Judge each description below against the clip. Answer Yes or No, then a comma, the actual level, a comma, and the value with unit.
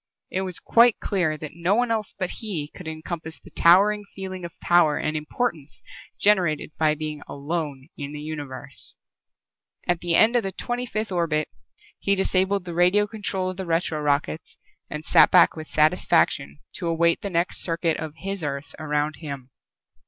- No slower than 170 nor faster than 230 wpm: Yes, average, 175 wpm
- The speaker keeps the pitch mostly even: No, average, 3.9 semitones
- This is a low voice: No, medium, 170 Hz